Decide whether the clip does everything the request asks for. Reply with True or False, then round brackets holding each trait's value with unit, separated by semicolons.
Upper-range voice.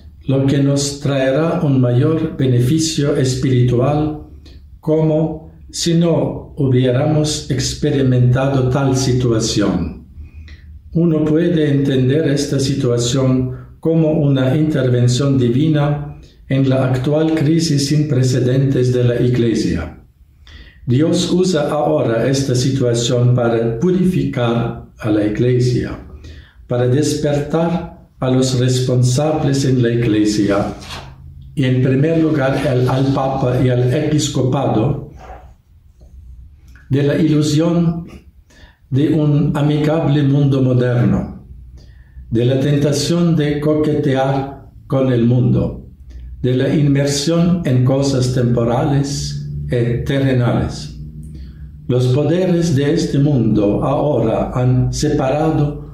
False (130 Hz)